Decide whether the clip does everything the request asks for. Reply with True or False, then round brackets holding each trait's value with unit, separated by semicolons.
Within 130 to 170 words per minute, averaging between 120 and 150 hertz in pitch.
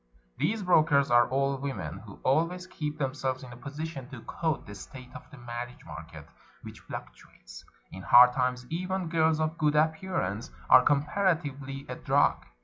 True (160 wpm; 140 Hz)